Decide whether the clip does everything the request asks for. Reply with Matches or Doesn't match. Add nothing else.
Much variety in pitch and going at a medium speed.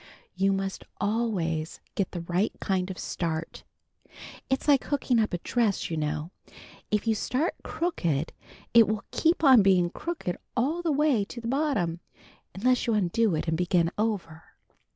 Matches